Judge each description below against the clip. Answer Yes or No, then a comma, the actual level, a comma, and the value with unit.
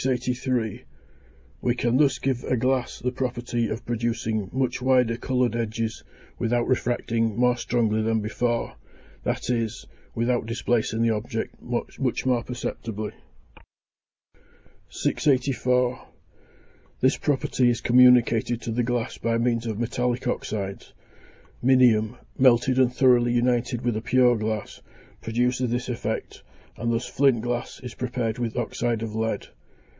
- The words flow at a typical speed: No, slow, 130 wpm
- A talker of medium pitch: No, low, 120 Hz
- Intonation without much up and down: Yes, narrow, 1.6 semitones